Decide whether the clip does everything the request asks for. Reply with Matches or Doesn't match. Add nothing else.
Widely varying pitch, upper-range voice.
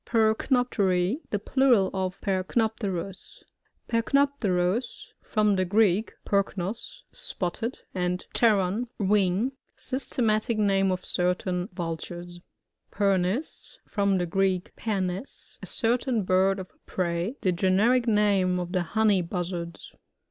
Doesn't match